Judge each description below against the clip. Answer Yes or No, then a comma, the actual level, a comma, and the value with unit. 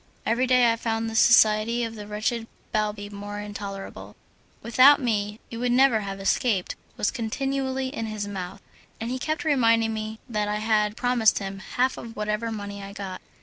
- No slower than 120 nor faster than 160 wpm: No, average, 180 wpm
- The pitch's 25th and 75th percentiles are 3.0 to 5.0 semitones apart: No, narrow, 2.6 semitones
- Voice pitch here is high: Yes, high, 220 Hz